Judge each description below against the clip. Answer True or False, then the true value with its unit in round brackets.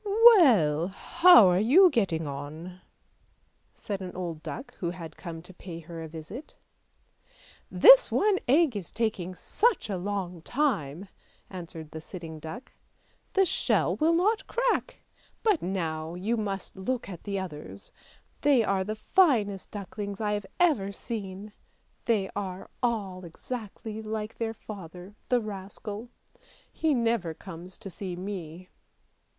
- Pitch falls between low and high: False (195 Hz)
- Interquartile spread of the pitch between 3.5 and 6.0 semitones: True (5.0 semitones)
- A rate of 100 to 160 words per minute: True (145 wpm)